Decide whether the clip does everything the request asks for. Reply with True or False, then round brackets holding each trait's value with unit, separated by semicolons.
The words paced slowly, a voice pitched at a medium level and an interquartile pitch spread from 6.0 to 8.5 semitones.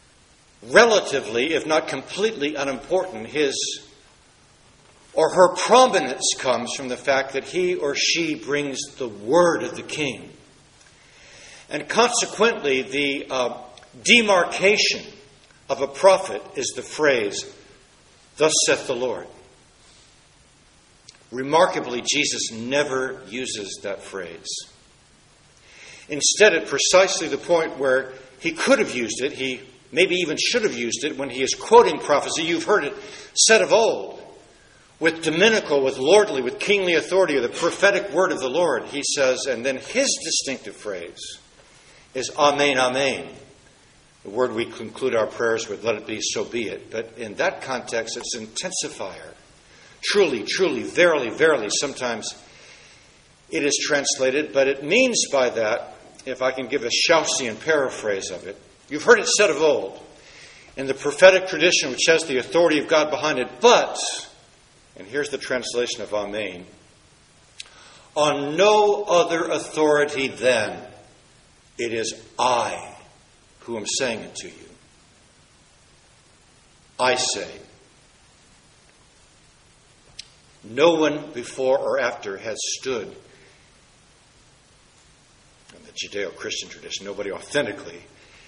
True (130 wpm; 150 Hz; 7.7 semitones)